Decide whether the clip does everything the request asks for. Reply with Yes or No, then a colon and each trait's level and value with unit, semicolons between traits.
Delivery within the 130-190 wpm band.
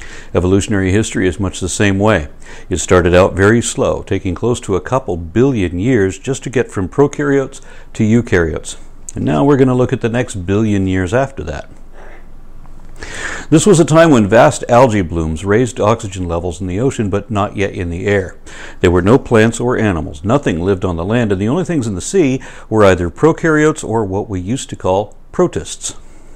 No: average, 200 wpm